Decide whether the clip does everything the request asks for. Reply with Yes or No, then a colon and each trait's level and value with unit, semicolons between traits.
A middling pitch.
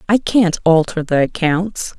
Yes: medium, 180 Hz